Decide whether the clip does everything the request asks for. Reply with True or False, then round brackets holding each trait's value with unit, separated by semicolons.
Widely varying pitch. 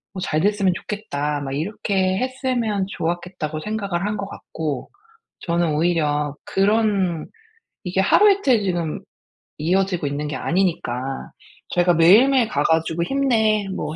False (4.6 semitones)